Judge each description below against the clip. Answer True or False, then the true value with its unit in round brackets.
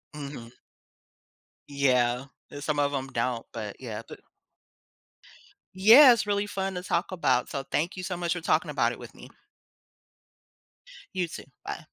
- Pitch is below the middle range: False (145 Hz)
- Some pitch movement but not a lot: False (6.5 semitones)